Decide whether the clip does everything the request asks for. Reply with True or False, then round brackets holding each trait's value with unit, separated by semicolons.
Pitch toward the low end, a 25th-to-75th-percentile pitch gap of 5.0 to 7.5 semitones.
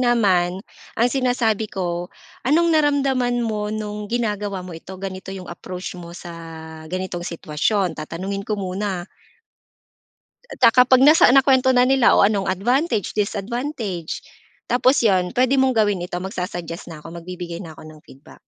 False (200 Hz; 5.4 semitones)